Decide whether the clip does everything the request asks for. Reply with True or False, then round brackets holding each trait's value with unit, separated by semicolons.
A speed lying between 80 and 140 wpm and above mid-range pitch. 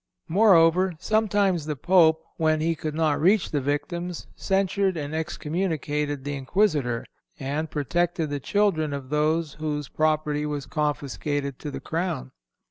False (135 wpm; 155 Hz)